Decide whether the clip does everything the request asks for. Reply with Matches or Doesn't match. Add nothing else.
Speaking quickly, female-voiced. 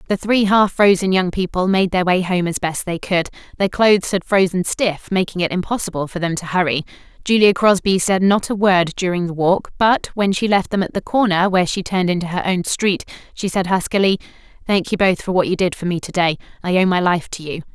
Matches